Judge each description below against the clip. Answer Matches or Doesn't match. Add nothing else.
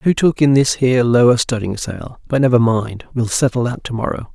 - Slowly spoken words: Doesn't match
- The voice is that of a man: Matches